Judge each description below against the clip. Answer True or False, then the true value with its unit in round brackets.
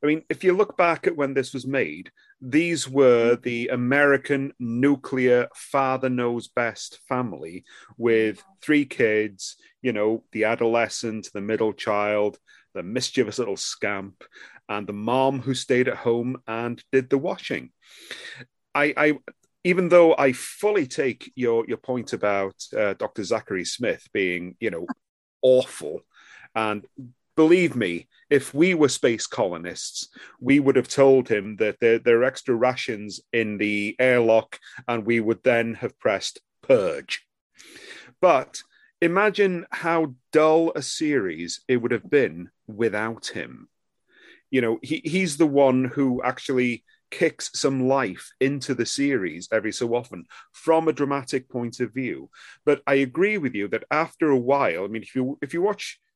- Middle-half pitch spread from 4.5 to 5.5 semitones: False (4.1 semitones)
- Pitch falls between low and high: False (130 Hz)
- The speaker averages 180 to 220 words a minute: False (155 wpm)